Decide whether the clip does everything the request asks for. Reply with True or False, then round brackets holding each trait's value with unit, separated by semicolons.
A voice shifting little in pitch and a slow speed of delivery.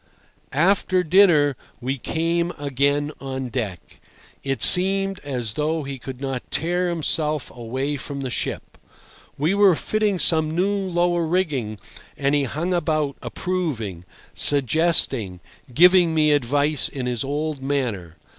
False (4.5 semitones; 130 wpm)